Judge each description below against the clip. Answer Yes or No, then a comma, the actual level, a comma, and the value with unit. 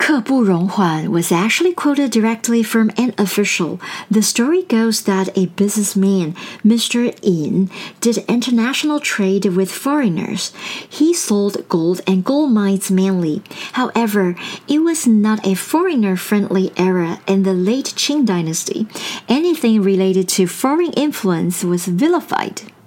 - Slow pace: Yes, slow, 130 wpm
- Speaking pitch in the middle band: No, high, 210 Hz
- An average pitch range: Yes, average, 4.4 semitones